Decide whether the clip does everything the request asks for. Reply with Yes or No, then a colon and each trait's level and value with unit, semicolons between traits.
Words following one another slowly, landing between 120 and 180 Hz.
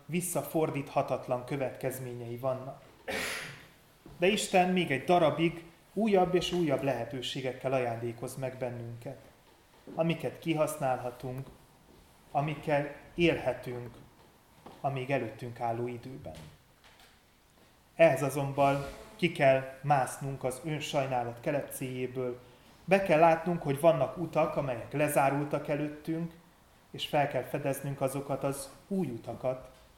Yes: slow, 100 wpm; medium, 140 Hz